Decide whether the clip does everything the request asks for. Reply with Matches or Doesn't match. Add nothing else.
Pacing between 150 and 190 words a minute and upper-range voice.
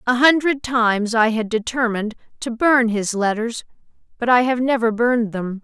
Matches